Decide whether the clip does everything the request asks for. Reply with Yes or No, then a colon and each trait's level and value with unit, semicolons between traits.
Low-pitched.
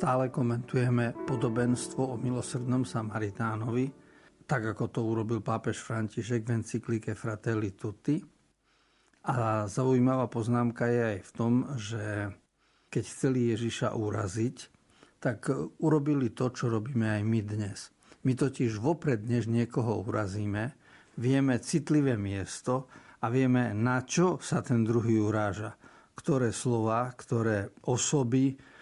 Yes: low, 120 Hz